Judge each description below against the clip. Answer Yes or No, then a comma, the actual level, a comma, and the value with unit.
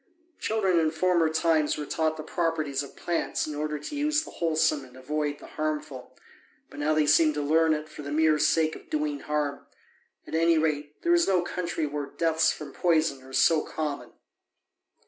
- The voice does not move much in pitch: Yes, narrow, 1.7 semitones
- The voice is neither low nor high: Yes, medium, 155 Hz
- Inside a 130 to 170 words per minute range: No, average, 190 wpm